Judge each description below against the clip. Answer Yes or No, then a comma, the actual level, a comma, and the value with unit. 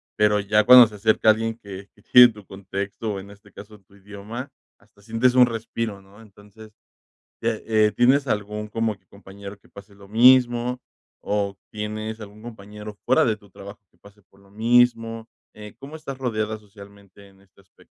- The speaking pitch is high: No, low, 105 Hz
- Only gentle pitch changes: Yes, narrow, 2.2 semitones